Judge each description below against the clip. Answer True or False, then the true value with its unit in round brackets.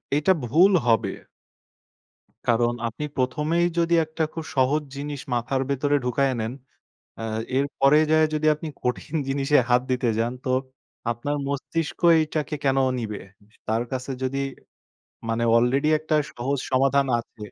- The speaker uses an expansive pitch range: False (3.4 semitones)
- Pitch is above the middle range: False (135 Hz)